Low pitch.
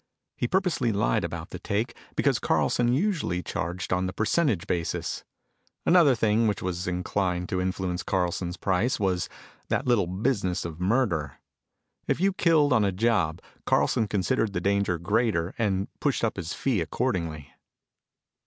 Yes: low, 100 Hz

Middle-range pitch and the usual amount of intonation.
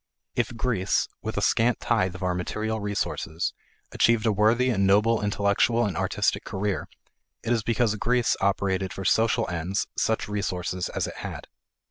No: low, 105 Hz; average, 3.2 semitones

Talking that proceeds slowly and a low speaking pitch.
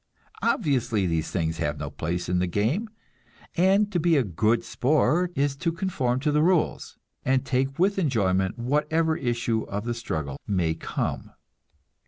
No: average, 160 wpm; low, 125 Hz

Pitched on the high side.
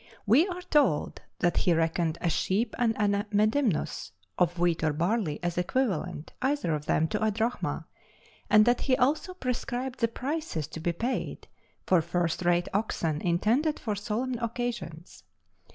Yes: high, 210 Hz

